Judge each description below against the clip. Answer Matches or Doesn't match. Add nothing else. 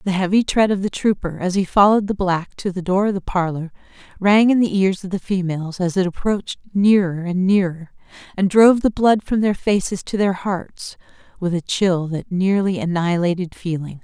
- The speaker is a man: Doesn't match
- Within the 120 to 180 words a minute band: Doesn't match